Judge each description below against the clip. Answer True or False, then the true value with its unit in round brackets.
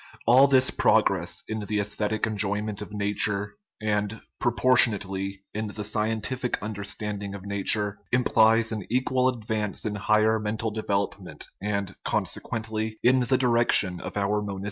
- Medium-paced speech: True (145 wpm)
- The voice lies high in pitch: False (105 Hz)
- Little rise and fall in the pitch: True (1.7 semitones)